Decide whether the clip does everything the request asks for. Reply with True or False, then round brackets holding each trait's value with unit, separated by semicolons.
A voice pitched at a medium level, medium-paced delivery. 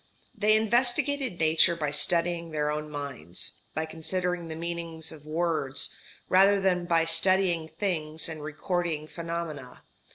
False (165 Hz; 130 wpm)